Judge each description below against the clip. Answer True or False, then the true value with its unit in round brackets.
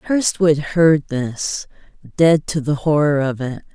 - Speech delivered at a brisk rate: False (145 wpm)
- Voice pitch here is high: False (150 Hz)